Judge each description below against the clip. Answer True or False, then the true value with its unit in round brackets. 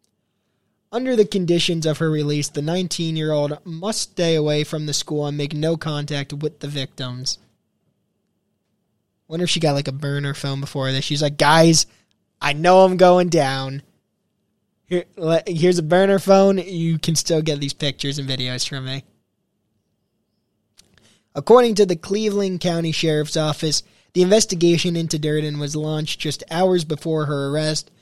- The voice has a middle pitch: True (155 Hz)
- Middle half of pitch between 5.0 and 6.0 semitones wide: False (3.4 semitones)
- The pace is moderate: True (155 wpm)